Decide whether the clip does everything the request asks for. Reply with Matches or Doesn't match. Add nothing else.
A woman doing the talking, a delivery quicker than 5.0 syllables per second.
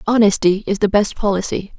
Matches